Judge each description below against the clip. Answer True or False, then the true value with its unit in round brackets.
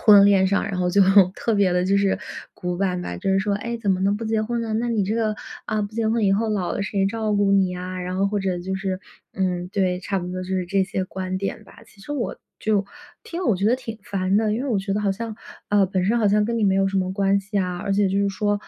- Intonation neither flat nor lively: False (2.2 semitones)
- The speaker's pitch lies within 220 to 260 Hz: False (200 Hz)